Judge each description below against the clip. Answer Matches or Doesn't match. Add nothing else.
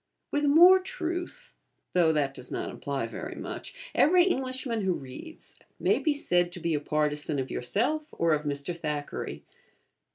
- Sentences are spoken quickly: Doesn't match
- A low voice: Doesn't match